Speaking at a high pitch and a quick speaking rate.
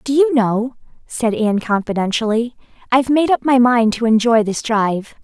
No: high, 235 Hz; average, 170 wpm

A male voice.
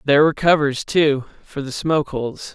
Yes: male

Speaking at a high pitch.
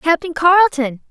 Yes: very high, 315 Hz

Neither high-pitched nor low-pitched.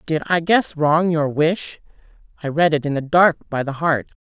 Yes: medium, 155 Hz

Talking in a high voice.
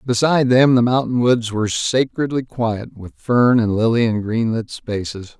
No: low, 115 Hz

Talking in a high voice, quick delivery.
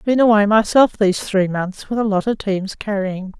Yes: high, 205 Hz; fast, 210 wpm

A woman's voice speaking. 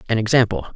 No: male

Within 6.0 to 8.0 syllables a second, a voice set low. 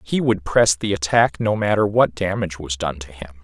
No: 5.3 syllables/s; very low, 95 Hz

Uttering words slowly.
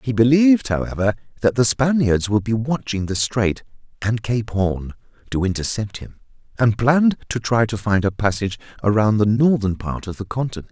No: average, 180 wpm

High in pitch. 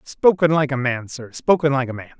No: medium, 140 Hz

